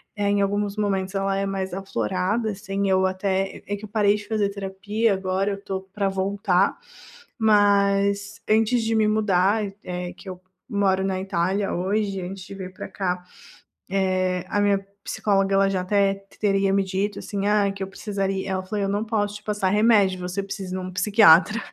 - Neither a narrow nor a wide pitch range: No, narrow, 1.4 semitones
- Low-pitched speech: No, high, 195 Hz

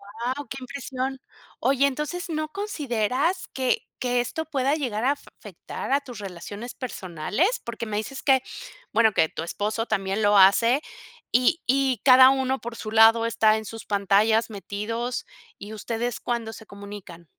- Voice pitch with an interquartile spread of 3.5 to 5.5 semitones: Yes, average, 4.0 semitones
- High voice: Yes, high, 235 Hz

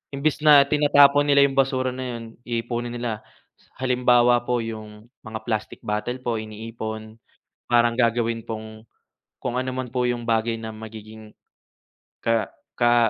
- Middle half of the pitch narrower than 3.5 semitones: Yes, narrow, 2.4 semitones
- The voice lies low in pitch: Yes, low, 120 Hz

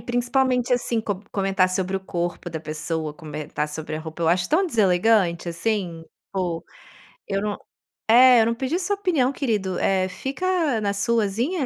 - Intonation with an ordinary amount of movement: No, wide, 6.1 semitones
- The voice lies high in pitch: Yes, high, 200 Hz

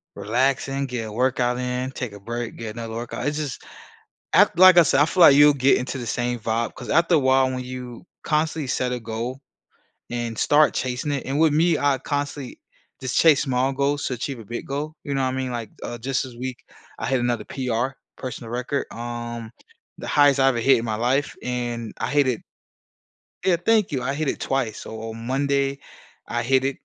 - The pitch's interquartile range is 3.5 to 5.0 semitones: No, average, 2.8 semitones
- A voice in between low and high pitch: No, low, 130 Hz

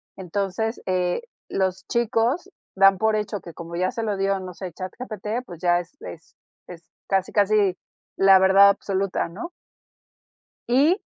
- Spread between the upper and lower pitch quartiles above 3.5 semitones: No, average, 2.8 semitones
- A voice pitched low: No, high, 195 Hz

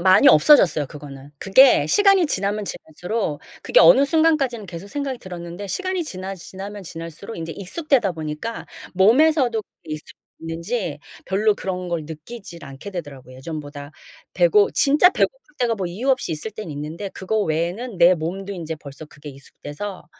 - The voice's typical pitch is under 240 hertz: Yes, high, 190 Hz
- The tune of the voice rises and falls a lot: Yes, wide, 6.8 semitones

